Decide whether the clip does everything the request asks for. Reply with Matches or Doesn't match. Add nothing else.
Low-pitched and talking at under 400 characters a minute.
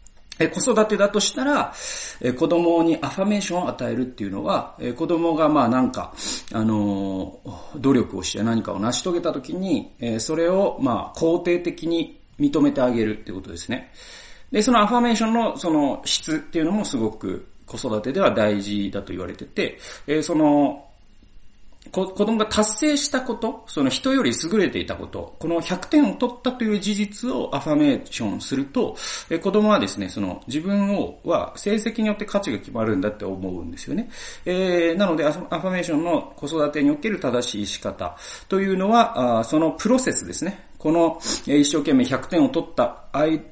Doesn't match